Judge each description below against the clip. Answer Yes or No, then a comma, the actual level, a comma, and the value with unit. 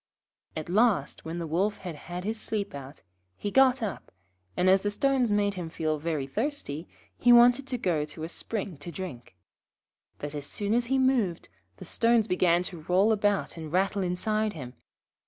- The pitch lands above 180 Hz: Yes, high, 190 Hz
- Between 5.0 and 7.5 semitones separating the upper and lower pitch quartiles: Yes, wide, 5.4 semitones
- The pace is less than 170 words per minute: No, average, 185 wpm